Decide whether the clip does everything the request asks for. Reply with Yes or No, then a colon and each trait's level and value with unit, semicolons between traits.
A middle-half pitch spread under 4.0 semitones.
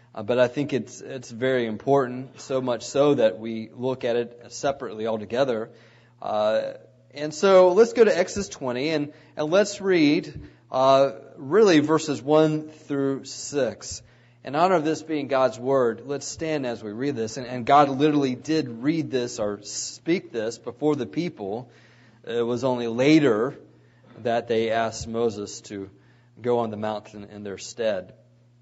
No: average, 4.3 semitones